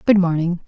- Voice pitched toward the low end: No, medium, 180 Hz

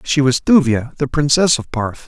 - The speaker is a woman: No, male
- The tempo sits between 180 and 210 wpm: Yes, fast, 205 wpm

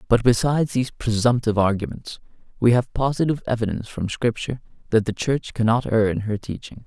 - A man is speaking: Yes, male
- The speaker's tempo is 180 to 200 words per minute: No, average, 165 wpm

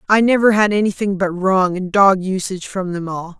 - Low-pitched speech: No, high, 190 Hz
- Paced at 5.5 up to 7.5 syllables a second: No, 5.3 syllables/s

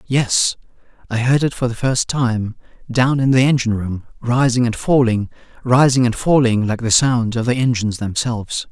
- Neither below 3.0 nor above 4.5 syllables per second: No, 5.0 syllables/s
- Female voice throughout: No, male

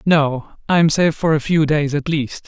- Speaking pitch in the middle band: Yes, medium, 150 Hz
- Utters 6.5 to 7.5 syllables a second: No, 5.1 syllables/s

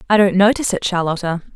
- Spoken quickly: No, average, 195 wpm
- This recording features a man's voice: No, female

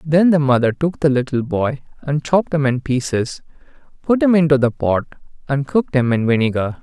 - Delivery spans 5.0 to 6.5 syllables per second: Yes, 5.5 syllables/s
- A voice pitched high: No, medium, 140 Hz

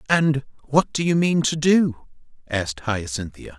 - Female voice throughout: No, male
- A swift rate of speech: No, average, 150 wpm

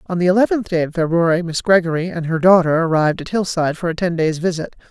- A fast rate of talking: Yes, fast, 230 wpm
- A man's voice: No, female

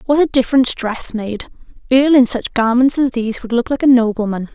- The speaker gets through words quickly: Yes, fast, 210 wpm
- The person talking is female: Yes, female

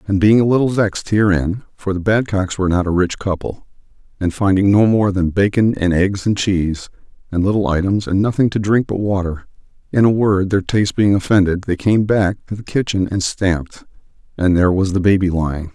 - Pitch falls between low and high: No, very low, 95 Hz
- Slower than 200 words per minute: No, fast, 205 wpm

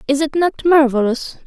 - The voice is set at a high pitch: Yes, very high, 285 Hz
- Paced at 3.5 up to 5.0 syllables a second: No, 5.5 syllables/s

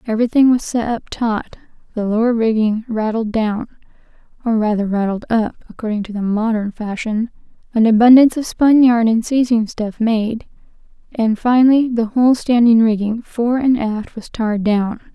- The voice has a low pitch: No, high, 225 Hz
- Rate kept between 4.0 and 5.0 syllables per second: Yes, 4.5 syllables/s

